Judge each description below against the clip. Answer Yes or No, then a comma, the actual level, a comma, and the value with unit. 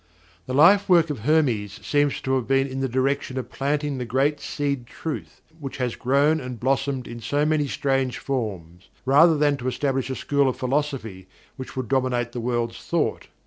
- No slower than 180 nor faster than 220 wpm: Yes, average, 185 wpm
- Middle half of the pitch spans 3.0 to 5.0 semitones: No, narrow, 2.6 semitones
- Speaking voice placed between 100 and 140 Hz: Yes, low, 135 Hz